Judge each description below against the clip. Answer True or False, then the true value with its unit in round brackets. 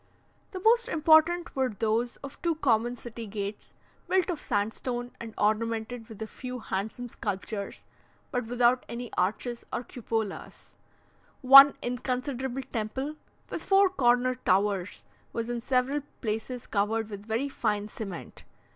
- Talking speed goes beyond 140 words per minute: False (135 wpm)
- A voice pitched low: False (240 Hz)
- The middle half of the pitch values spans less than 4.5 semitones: True (3.3 semitones)